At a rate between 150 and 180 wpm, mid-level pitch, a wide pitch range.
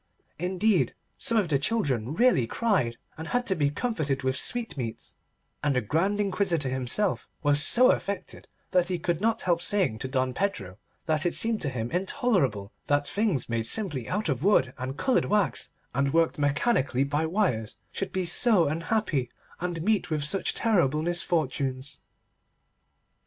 Yes: average, 160 wpm; medium, 160 Hz; wide, 7.1 semitones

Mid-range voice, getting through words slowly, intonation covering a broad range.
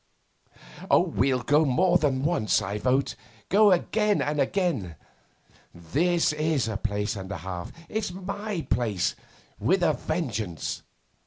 Yes: medium, 145 Hz; slow, 130 wpm; wide, 8.7 semitones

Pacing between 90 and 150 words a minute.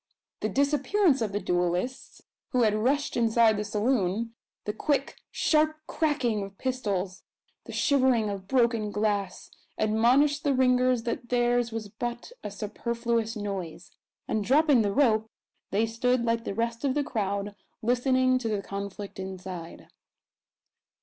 Yes: average, 140 wpm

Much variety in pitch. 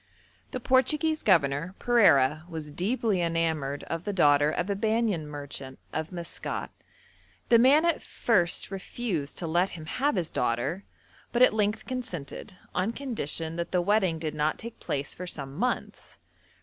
Yes: wide, 6.7 semitones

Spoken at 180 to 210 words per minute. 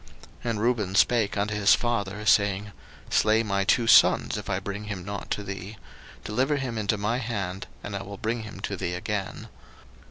Yes: average, 190 wpm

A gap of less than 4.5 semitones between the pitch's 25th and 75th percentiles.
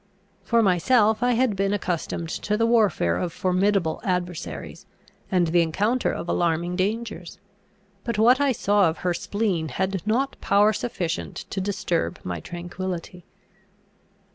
Yes: average, 3.8 semitones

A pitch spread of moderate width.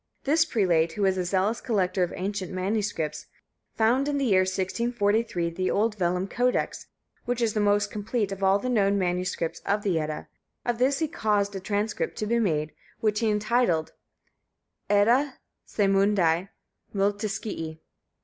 Yes: average, 3.3 semitones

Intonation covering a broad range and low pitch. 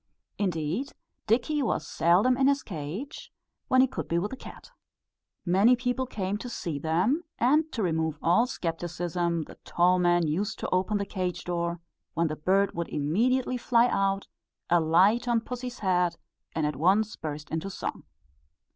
No: wide, 6.1 semitones; high, 190 Hz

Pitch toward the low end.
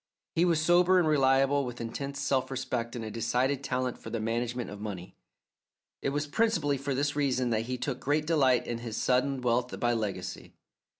Yes: low, 130 Hz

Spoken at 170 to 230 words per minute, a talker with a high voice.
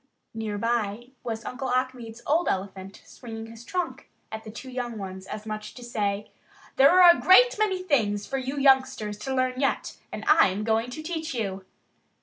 Yes: average, 185 wpm; high, 240 Hz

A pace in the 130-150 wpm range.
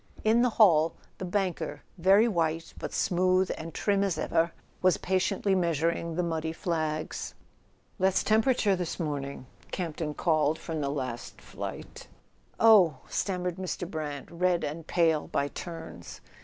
Yes: average, 140 wpm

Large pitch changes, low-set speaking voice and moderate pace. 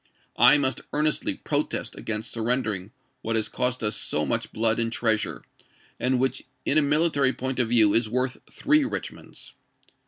No: average, 3.3 semitones; low, 125 Hz; average, 165 wpm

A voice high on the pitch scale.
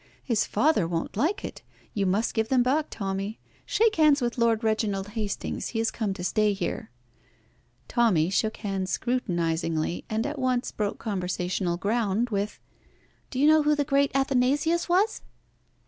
Yes: high, 225 Hz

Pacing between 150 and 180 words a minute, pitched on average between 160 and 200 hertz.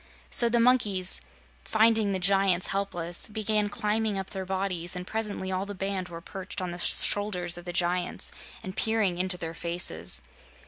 Yes: average, 170 wpm; high, 190 Hz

